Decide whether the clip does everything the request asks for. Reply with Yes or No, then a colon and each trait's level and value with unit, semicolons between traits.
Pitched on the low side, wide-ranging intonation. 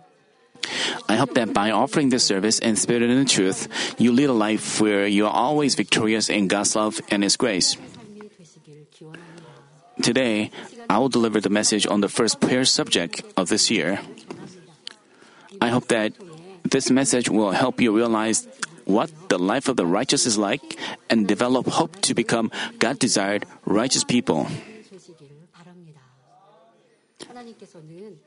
Yes: low, 125 Hz; wide, 7.2 semitones